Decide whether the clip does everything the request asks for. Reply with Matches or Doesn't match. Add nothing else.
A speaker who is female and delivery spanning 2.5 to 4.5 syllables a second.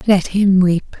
Doesn't match